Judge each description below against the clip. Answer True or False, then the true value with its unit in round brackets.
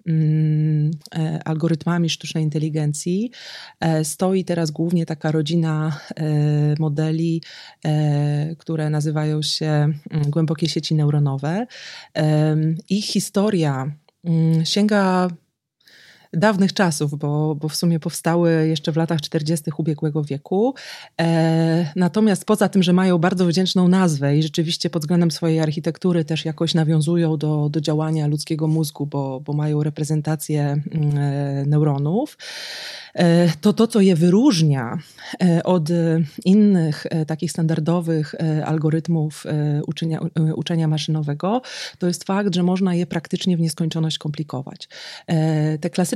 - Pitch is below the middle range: False (160 Hz)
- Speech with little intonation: True (2.3 semitones)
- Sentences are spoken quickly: False (120 wpm)